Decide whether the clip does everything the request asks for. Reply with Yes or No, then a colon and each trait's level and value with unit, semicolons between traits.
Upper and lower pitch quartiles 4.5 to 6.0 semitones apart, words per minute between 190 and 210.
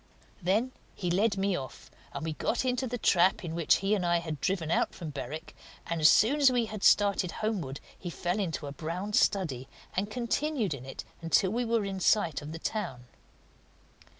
Yes: average, 4.9 semitones; average, 200 wpm